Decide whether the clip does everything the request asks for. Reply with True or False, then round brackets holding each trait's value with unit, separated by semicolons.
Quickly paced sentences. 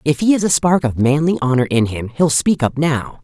True (260 wpm)